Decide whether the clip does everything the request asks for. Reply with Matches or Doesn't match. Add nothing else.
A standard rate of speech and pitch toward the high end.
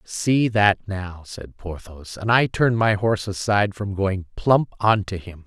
Doesn't match